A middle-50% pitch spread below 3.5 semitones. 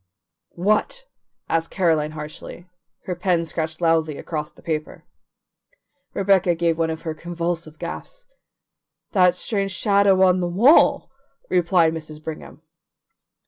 Yes: average, 2.7 semitones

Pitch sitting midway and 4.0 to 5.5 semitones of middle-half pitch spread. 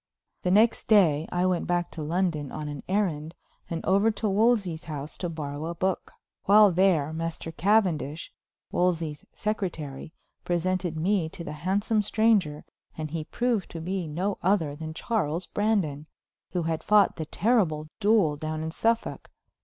Yes: medium, 175 Hz; average, 4.3 semitones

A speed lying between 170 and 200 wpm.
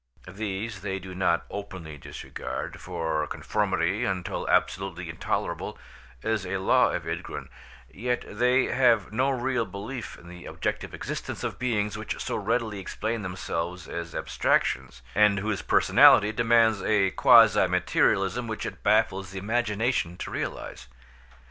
No: slow, 135 wpm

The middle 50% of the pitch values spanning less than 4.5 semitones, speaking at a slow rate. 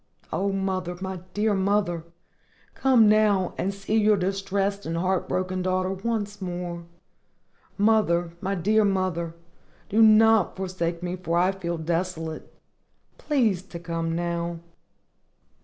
Yes: average, 2.8 semitones; slow, 125 wpm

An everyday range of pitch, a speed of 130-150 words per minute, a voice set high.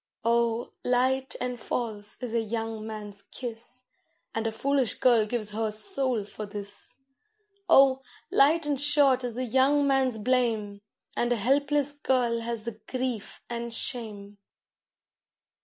Yes: average, 3.2 semitones; average, 140 wpm; high, 235 Hz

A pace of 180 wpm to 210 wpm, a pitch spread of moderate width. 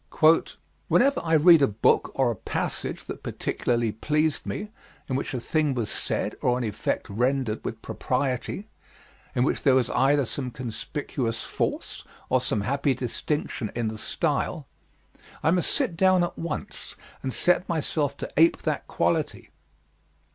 No: average, 155 wpm; average, 4.8 semitones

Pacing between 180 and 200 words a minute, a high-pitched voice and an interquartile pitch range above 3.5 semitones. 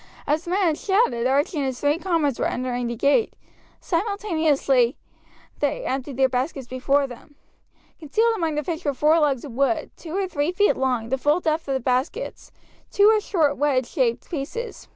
Yes: average, 190 wpm; very high, 290 Hz; average, 4.6 semitones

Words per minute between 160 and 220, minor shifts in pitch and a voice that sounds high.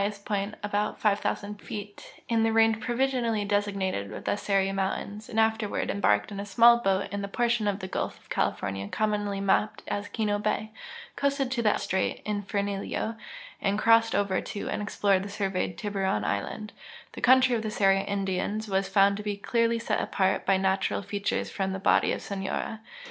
Yes: average, 185 wpm; narrow, 2.0 semitones; high, 205 Hz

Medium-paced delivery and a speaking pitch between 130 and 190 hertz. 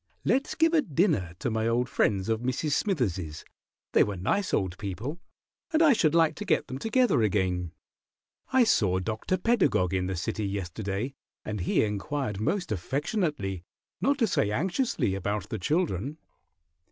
No: average, 160 wpm; low, 115 Hz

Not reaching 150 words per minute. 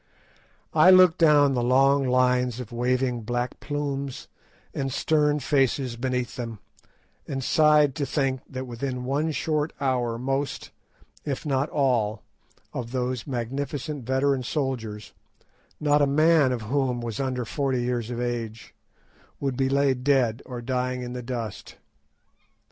Yes: average, 140 wpm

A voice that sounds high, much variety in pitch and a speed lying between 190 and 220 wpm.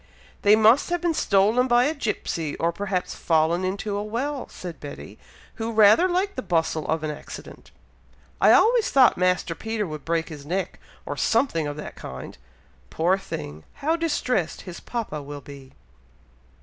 No: high, 195 Hz; wide, 7.3 semitones; average, 165 wpm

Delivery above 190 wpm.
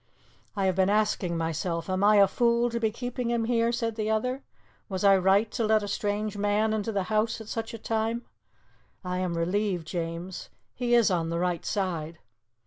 Yes: average, 200 wpm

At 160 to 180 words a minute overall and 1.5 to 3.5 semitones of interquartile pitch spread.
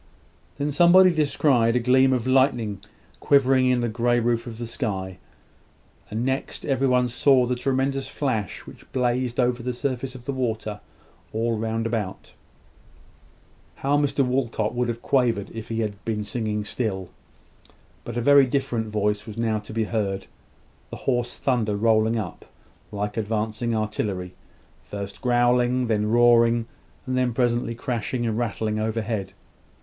No: average, 150 wpm; average, 2.7 semitones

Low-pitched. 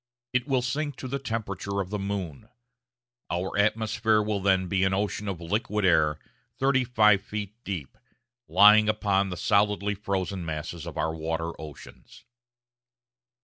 Yes: low, 100 Hz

